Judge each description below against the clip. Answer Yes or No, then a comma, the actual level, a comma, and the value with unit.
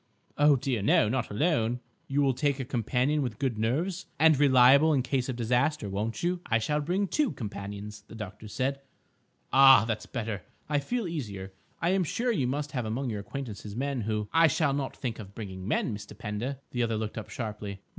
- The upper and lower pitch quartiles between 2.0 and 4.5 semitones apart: No, average, 5.0 semitones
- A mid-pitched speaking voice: No, low, 125 Hz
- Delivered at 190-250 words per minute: Yes, average, 200 wpm